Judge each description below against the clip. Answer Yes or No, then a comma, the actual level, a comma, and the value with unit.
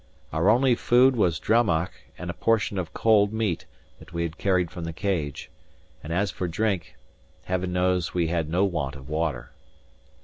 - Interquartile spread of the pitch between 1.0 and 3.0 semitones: No, average, 3.9 semitones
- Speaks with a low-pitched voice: Yes, very low, 90 Hz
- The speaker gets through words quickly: No, average, 175 wpm